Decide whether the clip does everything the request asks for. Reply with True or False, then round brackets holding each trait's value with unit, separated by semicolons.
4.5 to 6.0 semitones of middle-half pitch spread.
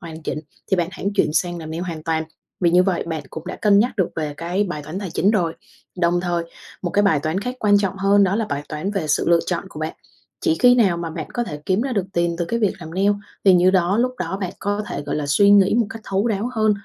False (3.4 semitones)